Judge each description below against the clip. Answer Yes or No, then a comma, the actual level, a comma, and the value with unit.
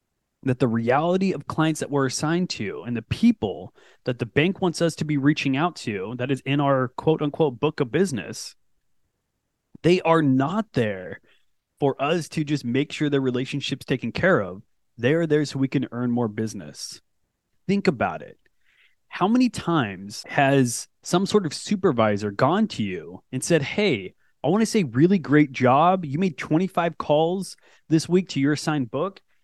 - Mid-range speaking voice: Yes, medium, 150 Hz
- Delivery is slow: No, average, 180 wpm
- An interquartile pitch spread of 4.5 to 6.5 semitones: Yes, average, 4.9 semitones